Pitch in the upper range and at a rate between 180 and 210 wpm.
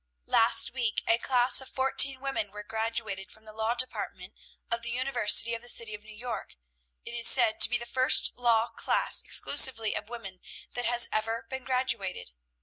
Yes: high, 235 Hz; average, 185 wpm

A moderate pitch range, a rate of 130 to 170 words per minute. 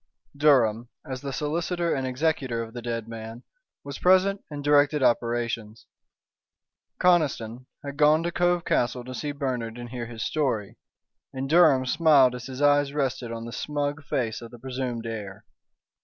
Yes: average, 4.0 semitones; average, 160 wpm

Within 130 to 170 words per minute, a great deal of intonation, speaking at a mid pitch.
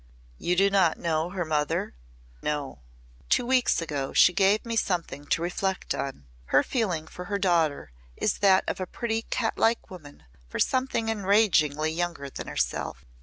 No: average, 165 wpm; average, 4.9 semitones; medium, 180 Hz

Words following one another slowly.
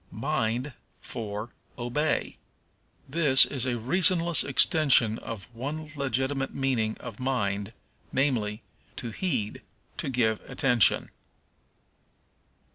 Yes: slow, 95 wpm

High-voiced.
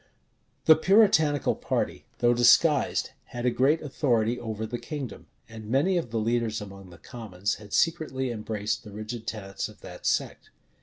No: low, 120 Hz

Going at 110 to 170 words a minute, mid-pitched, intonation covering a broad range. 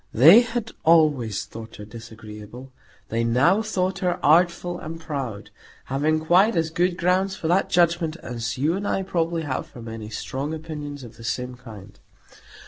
Yes: average, 165 wpm; medium, 155 Hz; wide, 7.0 semitones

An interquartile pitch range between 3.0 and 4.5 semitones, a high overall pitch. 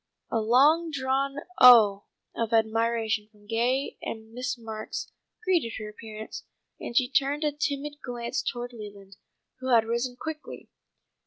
Yes: average, 3.5 semitones; high, 235 Hz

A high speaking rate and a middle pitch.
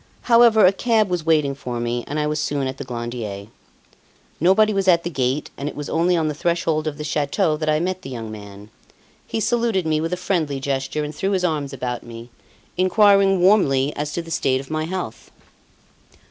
Yes: fast, 210 wpm; medium, 155 Hz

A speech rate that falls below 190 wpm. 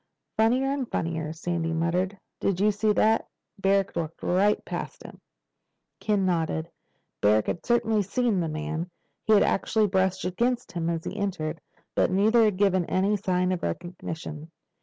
Yes: average, 160 wpm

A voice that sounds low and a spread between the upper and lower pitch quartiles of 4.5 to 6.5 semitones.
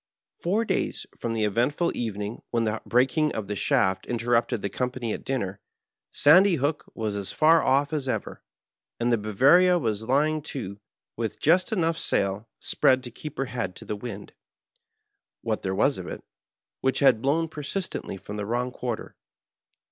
Yes: low, 125 Hz; wide, 5.6 semitones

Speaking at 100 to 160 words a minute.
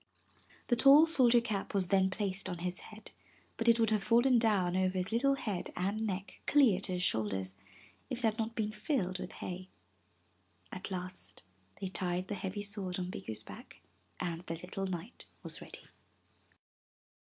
No: average, 175 wpm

